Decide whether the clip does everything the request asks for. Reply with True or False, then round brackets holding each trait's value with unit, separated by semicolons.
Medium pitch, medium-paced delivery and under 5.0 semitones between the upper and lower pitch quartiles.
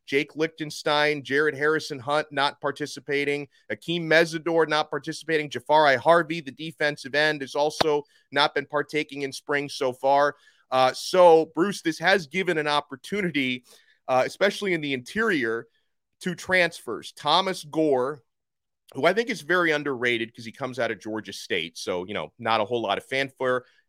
True (150 Hz; 160 wpm; 3.1 semitones)